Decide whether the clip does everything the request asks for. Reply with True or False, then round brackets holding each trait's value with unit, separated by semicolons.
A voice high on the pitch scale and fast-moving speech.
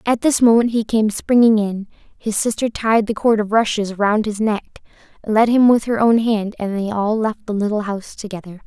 True (215 Hz; 215 wpm)